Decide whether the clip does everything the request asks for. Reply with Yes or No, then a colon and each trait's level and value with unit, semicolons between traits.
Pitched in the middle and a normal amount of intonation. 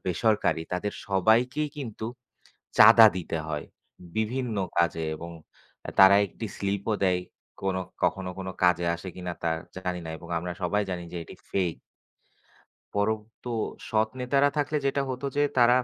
No: low, 100 Hz; average, 4.3 semitones